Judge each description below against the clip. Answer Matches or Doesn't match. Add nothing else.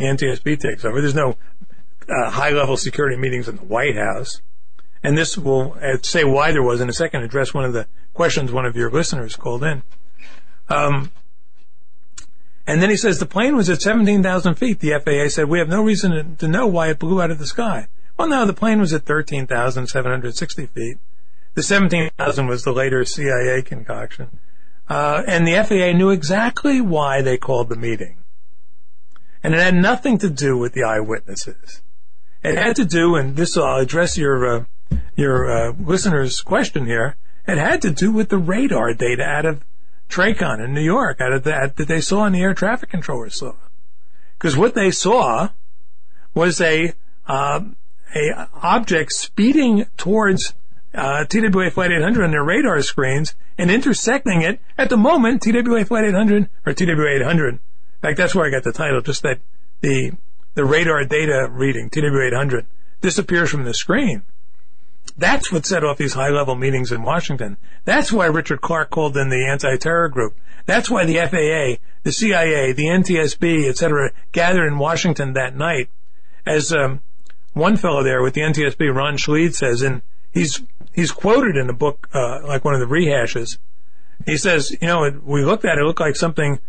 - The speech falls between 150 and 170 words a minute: Doesn't match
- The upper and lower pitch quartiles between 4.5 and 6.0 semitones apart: Matches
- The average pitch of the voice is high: Doesn't match